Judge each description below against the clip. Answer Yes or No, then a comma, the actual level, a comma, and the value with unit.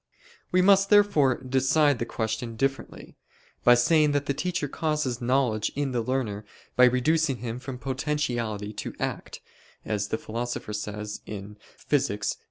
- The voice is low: Yes, low, 125 Hz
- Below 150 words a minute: Yes, average, 140 wpm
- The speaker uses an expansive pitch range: No, average, 4.7 semitones